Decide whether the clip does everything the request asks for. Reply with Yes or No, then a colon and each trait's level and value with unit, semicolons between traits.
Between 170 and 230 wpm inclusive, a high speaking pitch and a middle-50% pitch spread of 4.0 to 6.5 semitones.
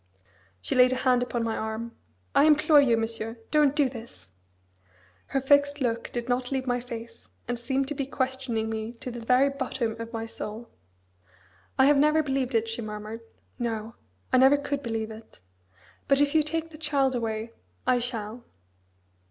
No: average, 175 wpm; high, 245 Hz; average, 3.3 semitones